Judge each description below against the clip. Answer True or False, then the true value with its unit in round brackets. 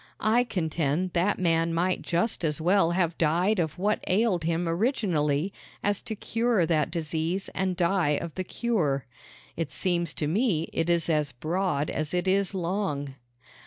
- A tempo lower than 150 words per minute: False (165 wpm)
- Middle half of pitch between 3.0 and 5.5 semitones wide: True (3.3 semitones)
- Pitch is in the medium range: True (175 Hz)